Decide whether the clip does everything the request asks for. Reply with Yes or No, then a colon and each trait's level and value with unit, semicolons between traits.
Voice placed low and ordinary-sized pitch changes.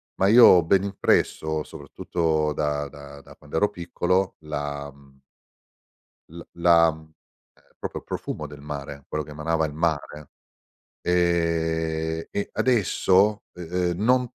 Yes: very low, 80 Hz; average, 3.0 semitones